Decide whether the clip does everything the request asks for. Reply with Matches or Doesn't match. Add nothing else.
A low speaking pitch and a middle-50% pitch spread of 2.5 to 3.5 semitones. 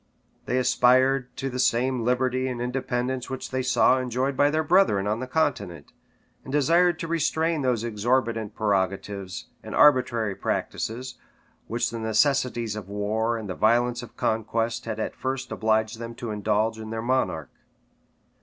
Matches